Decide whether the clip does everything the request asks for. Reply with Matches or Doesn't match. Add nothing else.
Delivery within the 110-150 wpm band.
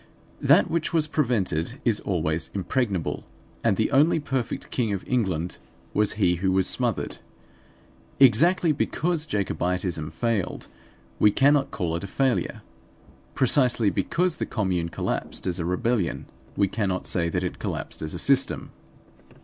Matches